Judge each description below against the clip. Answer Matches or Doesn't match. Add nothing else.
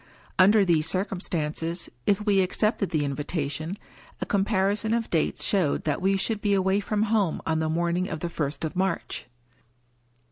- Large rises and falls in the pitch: Doesn't match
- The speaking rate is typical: Matches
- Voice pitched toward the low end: Doesn't match